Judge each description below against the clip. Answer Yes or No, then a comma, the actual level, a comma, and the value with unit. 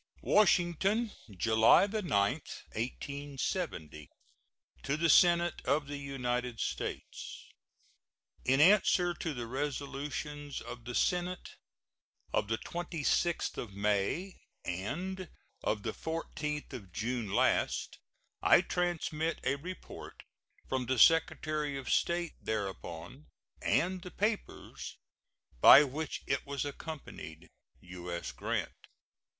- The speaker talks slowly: Yes, slow, 105 wpm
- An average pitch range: No, wide, 6.3 semitones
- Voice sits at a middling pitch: Yes, medium, 145 Hz